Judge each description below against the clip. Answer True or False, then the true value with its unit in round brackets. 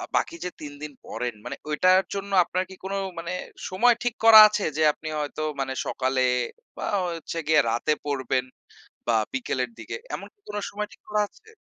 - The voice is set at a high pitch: False (165 Hz)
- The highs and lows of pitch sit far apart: True (7.4 semitones)